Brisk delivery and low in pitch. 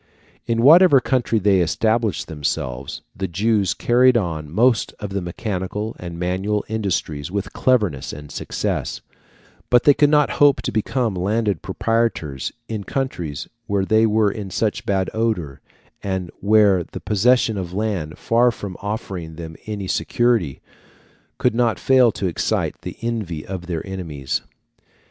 No: average, 145 wpm; low, 100 Hz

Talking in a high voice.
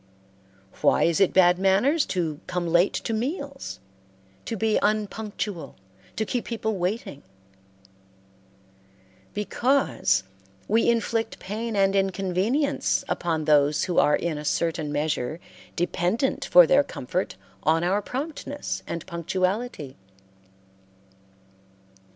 Yes: high, 195 Hz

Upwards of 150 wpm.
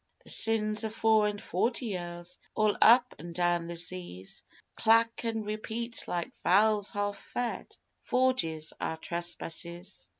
No: slow, 135 wpm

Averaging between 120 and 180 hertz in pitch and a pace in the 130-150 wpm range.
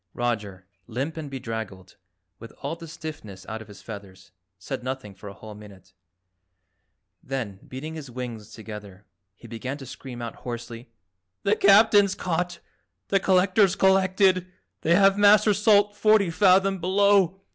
Yes: medium, 140 Hz; average, 145 wpm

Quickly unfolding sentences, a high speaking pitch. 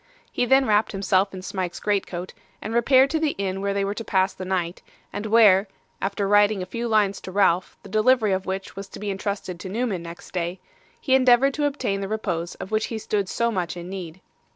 Yes: fast, 225 wpm; high, 200 Hz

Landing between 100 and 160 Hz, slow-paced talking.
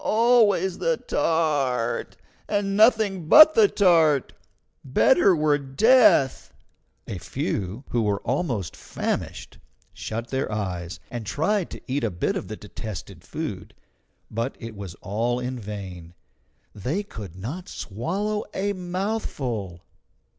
Yes: low, 135 Hz; slow, 125 wpm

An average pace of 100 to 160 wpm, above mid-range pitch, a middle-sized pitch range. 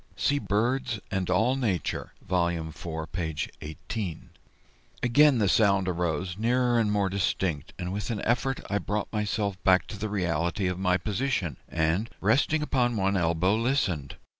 No: average, 155 wpm; low, 100 Hz; average, 4.6 semitones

